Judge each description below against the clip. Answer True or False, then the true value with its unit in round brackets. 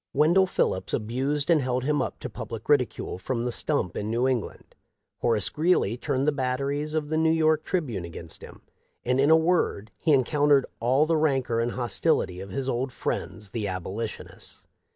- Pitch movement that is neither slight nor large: True (4.8 semitones)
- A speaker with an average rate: True (180 wpm)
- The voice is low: True (130 Hz)